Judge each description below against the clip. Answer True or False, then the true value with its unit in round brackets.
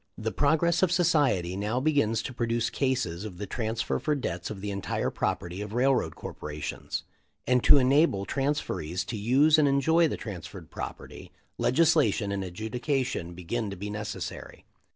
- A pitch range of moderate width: False (6.2 semitones)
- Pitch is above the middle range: False (115 Hz)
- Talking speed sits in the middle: True (155 wpm)